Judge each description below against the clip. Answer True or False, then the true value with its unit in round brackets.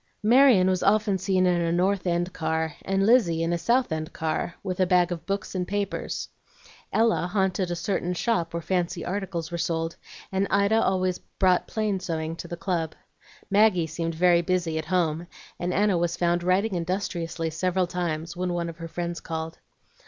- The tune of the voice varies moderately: False (2.3 semitones)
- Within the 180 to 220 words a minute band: True (185 wpm)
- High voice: False (180 Hz)